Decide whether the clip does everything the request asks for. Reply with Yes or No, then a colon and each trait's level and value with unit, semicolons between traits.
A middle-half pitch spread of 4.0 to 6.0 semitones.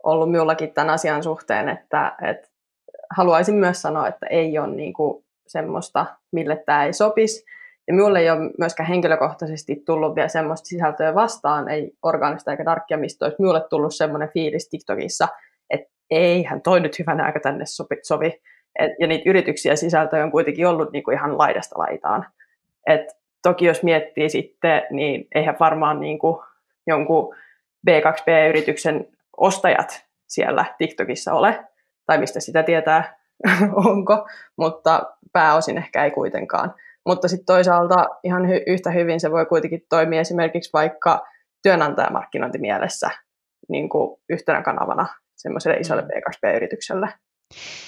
No: narrow, 2.5 semitones